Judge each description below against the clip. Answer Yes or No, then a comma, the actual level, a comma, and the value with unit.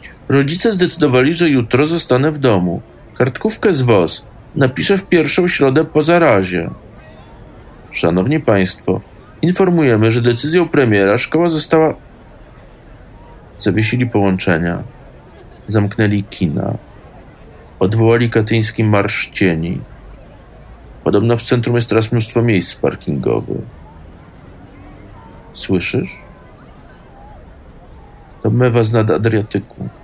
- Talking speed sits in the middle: No, slow, 90 wpm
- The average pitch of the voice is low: Yes, low, 115 Hz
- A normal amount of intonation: No, wide, 6.6 semitones